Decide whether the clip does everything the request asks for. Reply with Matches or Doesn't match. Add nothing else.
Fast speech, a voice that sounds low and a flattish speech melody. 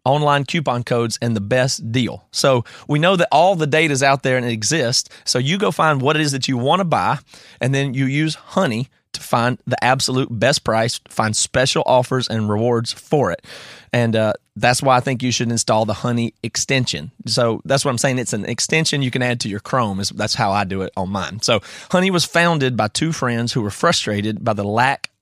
Doesn't match